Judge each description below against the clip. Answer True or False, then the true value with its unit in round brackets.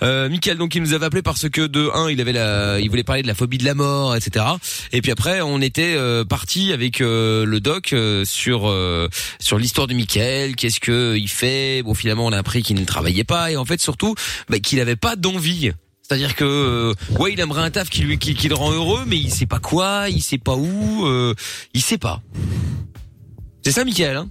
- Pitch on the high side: False (125 Hz)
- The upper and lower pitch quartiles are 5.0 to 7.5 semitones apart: True (5.5 semitones)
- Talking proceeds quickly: True (235 wpm)